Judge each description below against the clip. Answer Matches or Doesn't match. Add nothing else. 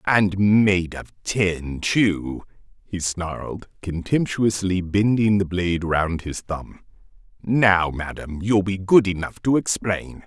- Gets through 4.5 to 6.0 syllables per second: Doesn't match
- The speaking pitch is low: Matches